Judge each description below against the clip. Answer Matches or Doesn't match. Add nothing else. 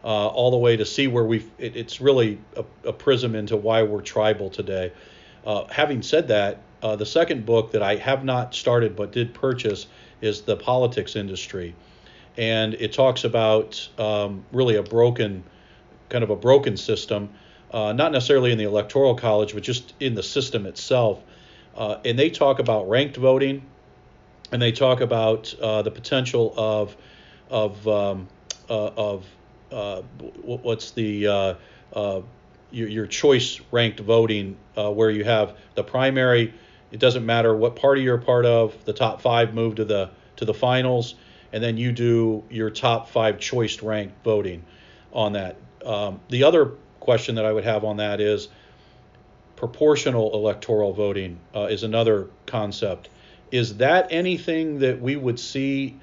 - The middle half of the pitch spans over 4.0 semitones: Doesn't match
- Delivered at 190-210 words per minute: Doesn't match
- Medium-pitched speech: Doesn't match